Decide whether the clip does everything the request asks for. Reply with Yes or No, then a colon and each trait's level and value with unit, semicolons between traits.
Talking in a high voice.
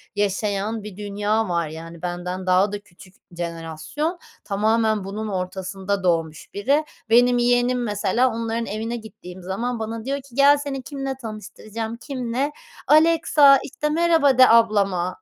Yes: high, 220 Hz